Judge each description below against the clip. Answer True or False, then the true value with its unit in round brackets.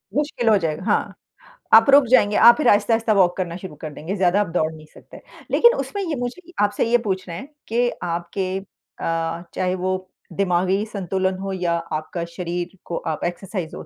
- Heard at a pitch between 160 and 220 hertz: True (190 Hz)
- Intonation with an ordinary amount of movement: True (3.8 semitones)